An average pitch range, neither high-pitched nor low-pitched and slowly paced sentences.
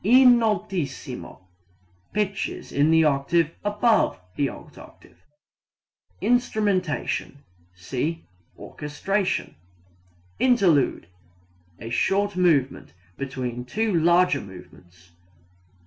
No: wide, 6.9 semitones; medium, 165 Hz; slow, 80 wpm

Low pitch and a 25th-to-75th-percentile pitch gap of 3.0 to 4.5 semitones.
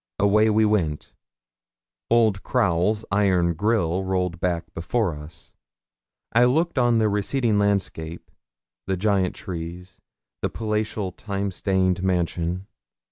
Yes: very low, 95 Hz; average, 3.6 semitones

